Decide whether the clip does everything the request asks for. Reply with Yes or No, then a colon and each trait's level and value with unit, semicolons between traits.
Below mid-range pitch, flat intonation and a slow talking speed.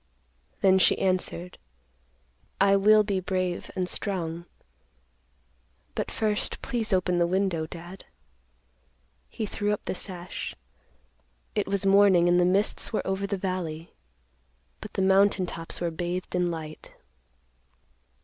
No: medium, 185 Hz; narrow, 2.2 semitones; slow, 130 wpm